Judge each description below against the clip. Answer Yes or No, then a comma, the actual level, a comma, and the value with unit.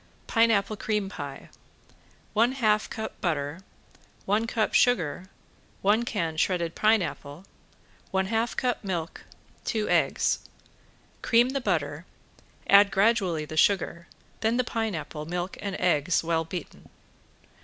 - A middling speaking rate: No, slow, 120 wpm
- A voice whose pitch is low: No, high, 195 Hz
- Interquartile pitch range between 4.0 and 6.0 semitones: Yes, average, 5.1 semitones